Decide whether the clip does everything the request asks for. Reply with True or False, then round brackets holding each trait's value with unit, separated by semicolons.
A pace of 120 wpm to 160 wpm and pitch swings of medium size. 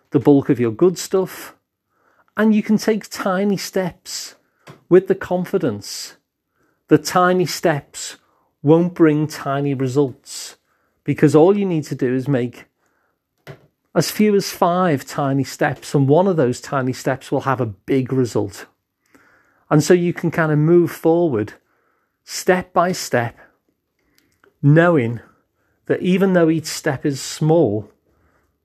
True (140 wpm; 4.9 semitones)